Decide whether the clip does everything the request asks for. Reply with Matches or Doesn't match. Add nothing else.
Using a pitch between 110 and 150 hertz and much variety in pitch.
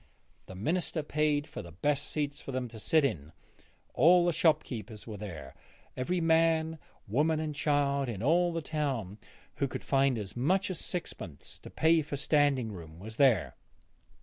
Matches